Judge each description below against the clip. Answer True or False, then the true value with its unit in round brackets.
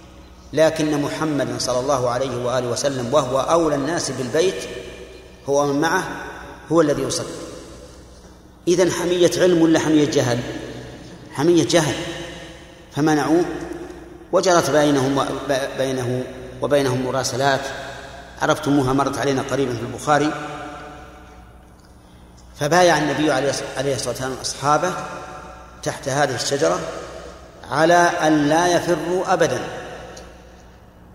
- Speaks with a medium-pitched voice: True (145 Hz)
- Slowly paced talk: False (100 wpm)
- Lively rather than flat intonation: False (4.2 semitones)